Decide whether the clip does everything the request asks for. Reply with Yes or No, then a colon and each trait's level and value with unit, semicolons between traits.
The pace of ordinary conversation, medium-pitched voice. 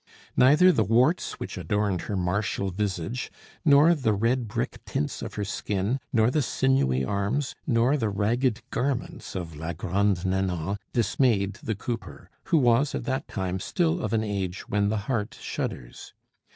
No: average, 160 wpm; low, 105 Hz